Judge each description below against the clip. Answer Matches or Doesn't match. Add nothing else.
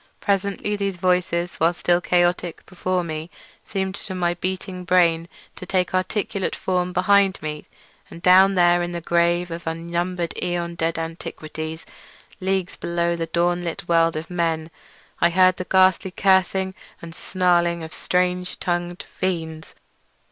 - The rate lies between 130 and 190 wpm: Matches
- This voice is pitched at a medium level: Matches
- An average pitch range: Doesn't match